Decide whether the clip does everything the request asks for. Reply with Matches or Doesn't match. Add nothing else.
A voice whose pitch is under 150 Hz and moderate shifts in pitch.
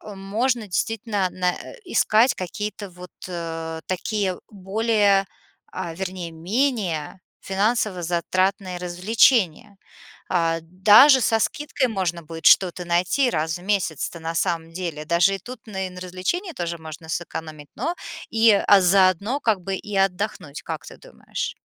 Doesn't match